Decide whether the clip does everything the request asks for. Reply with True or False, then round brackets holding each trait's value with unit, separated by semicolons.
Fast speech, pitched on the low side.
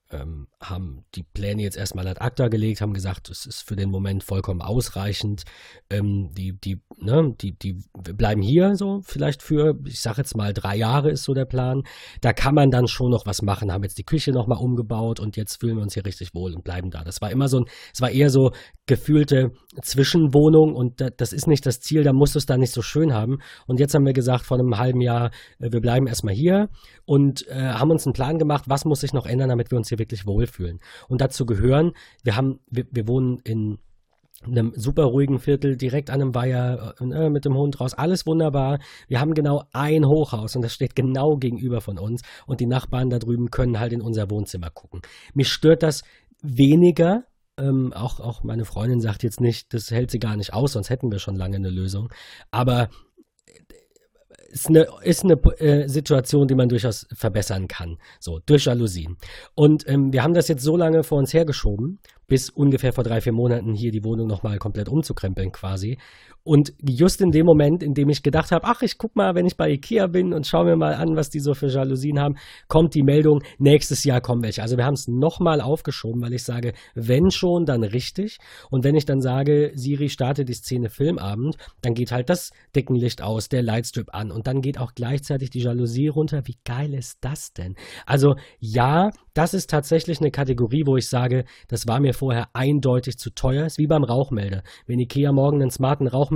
True (210 wpm; 130 Hz)